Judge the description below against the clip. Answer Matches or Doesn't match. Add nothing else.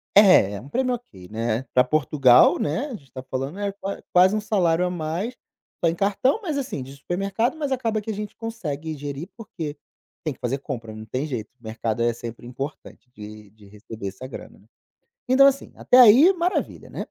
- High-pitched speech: Doesn't match